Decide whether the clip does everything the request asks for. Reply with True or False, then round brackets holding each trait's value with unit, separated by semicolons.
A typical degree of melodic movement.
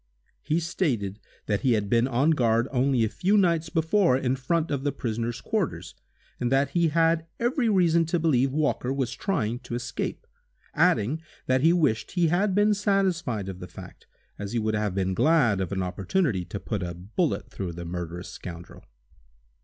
False (7.8 semitones)